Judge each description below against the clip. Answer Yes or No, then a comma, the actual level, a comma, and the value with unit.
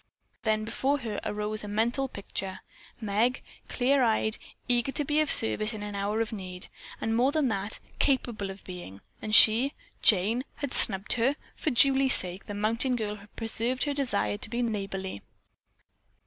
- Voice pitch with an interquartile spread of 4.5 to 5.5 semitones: No, average, 3.8 semitones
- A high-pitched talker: Yes, high, 220 Hz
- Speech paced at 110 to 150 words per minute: No, average, 175 wpm